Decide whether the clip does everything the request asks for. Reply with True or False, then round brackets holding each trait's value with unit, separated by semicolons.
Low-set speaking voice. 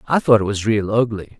True (110 Hz)